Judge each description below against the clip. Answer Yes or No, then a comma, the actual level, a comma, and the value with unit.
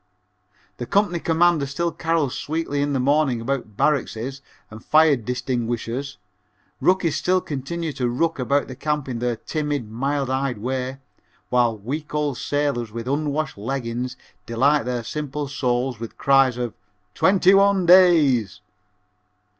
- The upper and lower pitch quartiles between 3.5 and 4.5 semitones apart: Yes, average, 3.8 semitones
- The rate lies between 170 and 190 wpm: No, average, 140 wpm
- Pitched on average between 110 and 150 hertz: Yes, low, 135 Hz